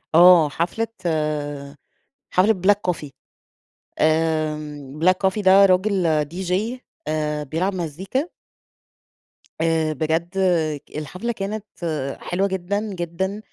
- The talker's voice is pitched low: No, medium, 170 Hz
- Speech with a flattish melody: No, average, 3.7 semitones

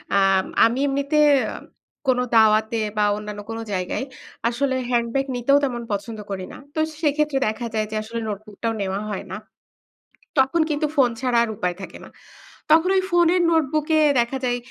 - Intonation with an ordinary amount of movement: Yes, average, 4.8 semitones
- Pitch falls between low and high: No, high, 240 Hz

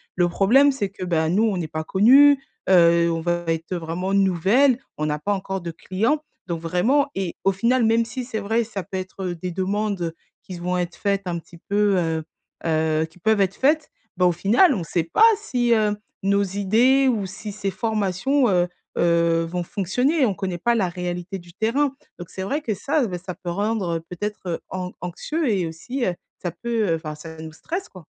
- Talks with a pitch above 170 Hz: Yes, high, 190 Hz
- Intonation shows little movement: No, average, 4.6 semitones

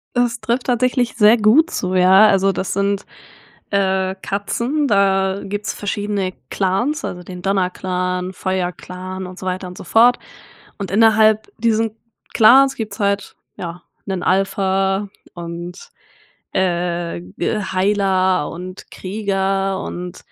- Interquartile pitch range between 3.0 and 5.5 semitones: No, narrow, 2.6 semitones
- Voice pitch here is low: No, high, 195 Hz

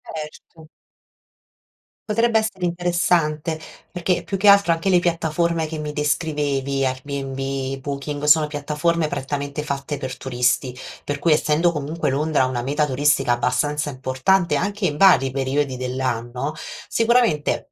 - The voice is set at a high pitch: No, medium, 150 Hz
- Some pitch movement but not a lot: Yes, average, 3.8 semitones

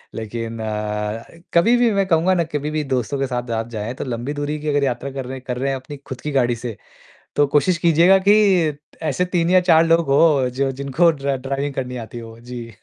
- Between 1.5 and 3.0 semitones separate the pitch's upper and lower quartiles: No, average, 4.3 semitones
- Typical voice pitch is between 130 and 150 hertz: Yes, low, 135 Hz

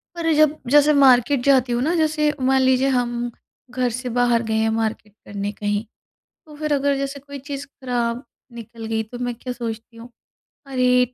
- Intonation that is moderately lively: Yes, average, 3.2 semitones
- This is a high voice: Yes, very high, 250 Hz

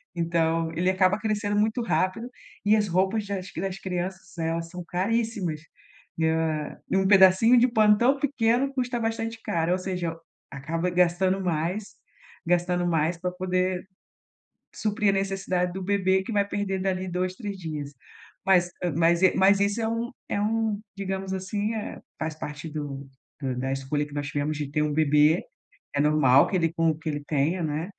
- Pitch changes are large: No, average, 3.8 semitones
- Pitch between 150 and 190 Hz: Yes, medium, 185 Hz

